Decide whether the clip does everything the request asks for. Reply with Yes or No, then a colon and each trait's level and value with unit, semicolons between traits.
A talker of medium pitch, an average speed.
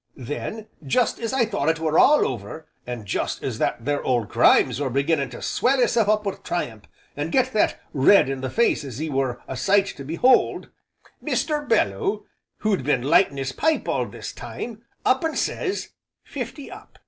Yes: medium, 160 Hz; average, 185 wpm